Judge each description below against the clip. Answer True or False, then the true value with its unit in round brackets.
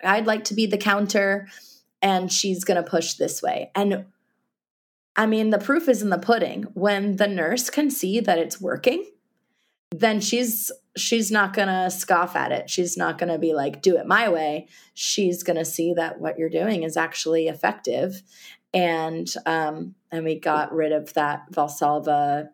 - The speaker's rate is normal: True (185 wpm)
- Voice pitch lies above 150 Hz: True (185 Hz)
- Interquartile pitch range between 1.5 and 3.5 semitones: False (4.5 semitones)